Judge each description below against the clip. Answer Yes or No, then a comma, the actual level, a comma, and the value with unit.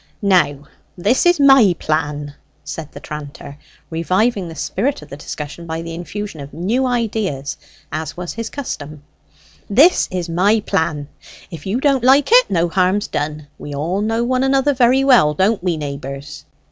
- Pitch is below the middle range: No, medium, 180 Hz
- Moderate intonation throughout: No, wide, 7.8 semitones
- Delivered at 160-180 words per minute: Yes, average, 165 wpm